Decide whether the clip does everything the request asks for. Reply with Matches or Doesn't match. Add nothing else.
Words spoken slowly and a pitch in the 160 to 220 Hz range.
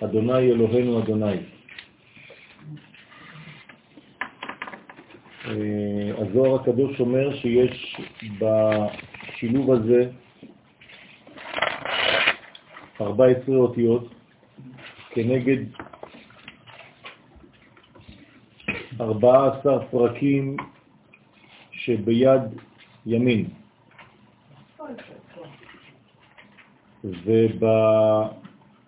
Doesn't match